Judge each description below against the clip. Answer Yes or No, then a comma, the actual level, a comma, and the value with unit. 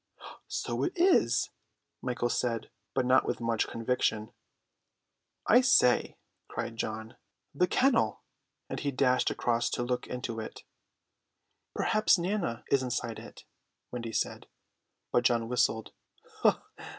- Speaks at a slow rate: Yes, slow, 120 wpm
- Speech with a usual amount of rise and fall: Yes, average, 3.3 semitones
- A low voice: Yes, low, 125 Hz